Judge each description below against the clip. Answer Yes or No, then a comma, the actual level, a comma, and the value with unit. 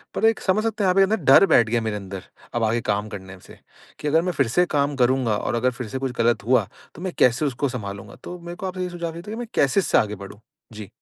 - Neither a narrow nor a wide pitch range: No, wide, 8.2 semitones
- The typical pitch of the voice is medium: No, low, 130 Hz